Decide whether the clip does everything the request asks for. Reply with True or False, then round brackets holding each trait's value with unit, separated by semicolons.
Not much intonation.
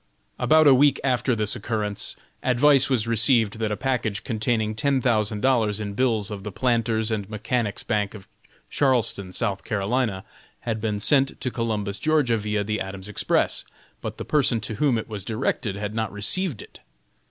False (3.3 semitones)